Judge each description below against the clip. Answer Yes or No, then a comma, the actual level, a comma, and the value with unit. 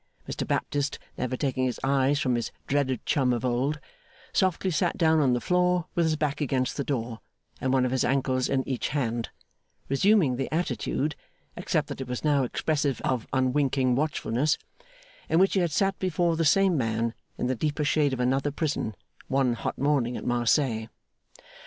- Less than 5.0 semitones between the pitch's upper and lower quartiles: Yes, average, 3.4 semitones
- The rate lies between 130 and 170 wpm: No, average, 180 wpm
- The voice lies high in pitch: No, low, 135 Hz